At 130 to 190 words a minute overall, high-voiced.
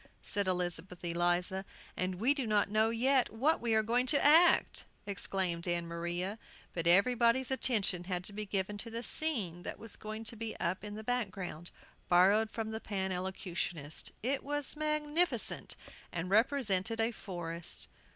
Yes: average, 155 wpm; high, 205 Hz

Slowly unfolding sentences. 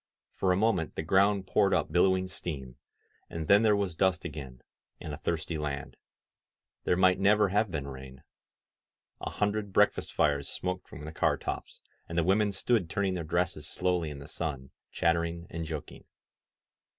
No: average, 170 wpm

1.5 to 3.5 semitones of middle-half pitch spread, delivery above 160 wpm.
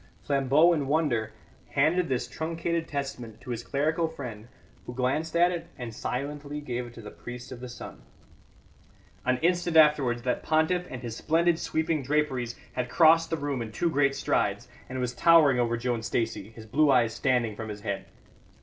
No: average, 4.7 semitones; average, 180 wpm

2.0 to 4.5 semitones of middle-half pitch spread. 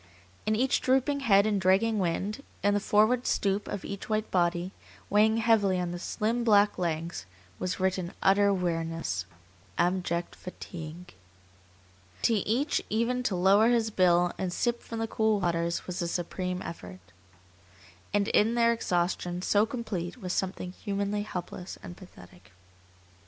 Yes: average, 3.7 semitones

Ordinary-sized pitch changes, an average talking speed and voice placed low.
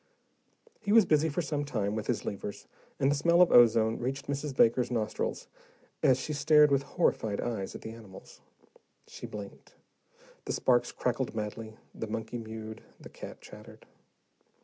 Yes: average, 4.6 semitones; average, 160 wpm; low, 120 Hz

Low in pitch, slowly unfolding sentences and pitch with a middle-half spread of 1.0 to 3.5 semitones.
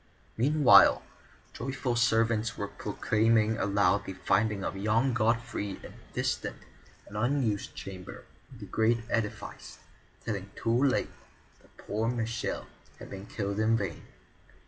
Yes: low, 110 Hz; slow, 130 wpm; narrow, 2.5 semitones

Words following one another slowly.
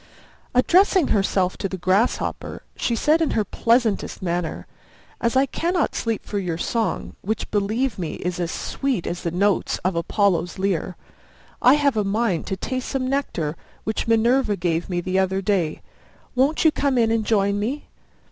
No: average, 170 wpm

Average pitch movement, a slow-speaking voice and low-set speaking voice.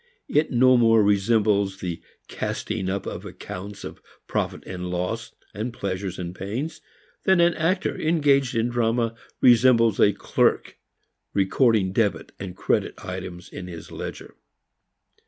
Yes: average, 4.6 semitones; slow, 130 wpm; low, 110 Hz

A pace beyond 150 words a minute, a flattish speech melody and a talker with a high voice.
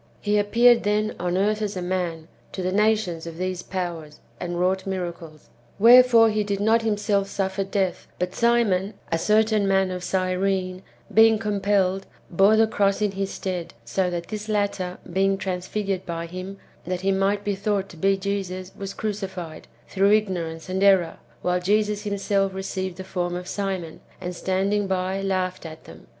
Yes: average, 170 wpm; narrow, 2.1 semitones; high, 195 Hz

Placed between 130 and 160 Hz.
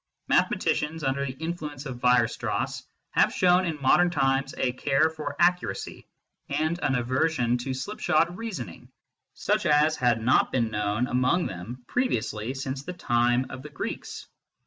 Yes: low, 135 Hz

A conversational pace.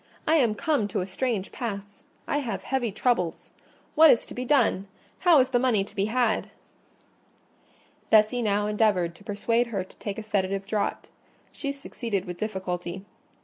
Yes: average, 170 wpm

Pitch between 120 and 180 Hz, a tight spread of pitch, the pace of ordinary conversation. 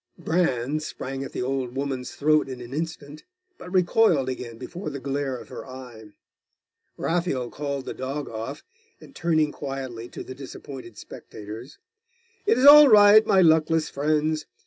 No: medium, 140 Hz; average, 3.8 semitones; average, 155 wpm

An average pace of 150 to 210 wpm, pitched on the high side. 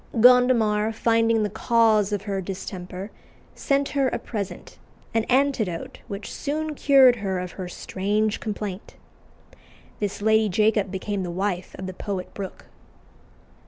No: slow, 135 wpm; high, 210 Hz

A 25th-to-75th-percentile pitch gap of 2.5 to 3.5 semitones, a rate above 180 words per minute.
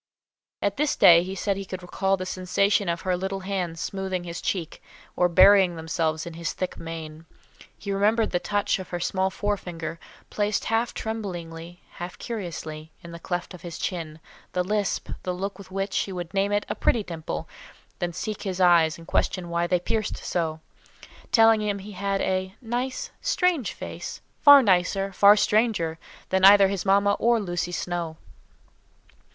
No: average, 2.9 semitones; average, 175 wpm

